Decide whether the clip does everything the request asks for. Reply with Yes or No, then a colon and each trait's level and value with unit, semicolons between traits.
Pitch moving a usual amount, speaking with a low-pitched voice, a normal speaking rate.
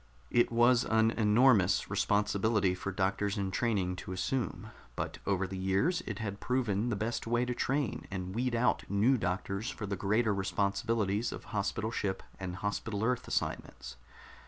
Yes: average, 3.4 semitones; low, 105 Hz; average, 160 wpm